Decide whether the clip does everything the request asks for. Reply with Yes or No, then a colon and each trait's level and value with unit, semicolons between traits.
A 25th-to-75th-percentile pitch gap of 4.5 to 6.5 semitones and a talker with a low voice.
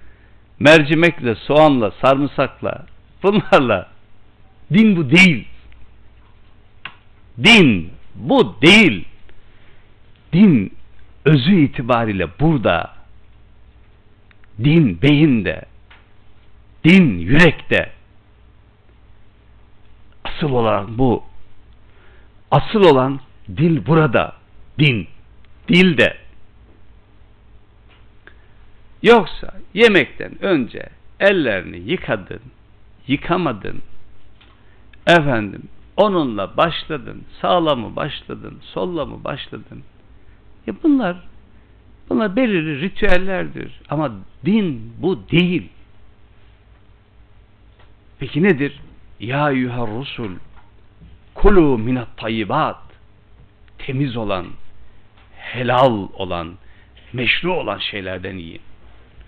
Yes: average, 5.1 semitones; low, 105 Hz